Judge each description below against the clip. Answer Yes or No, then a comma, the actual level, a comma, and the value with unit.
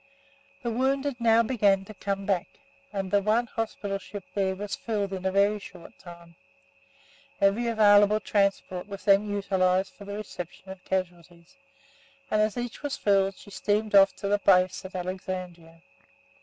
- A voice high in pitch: Yes, high, 200 Hz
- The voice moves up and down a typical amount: No, narrow, 2.2 semitones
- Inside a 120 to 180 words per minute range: Yes, average, 160 wpm